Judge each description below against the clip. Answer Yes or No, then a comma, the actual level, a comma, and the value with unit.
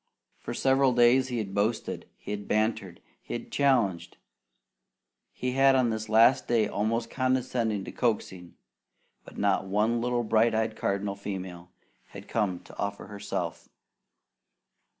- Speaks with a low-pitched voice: Yes, low, 110 Hz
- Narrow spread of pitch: No, average, 3.3 semitones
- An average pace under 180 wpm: Yes, average, 140 wpm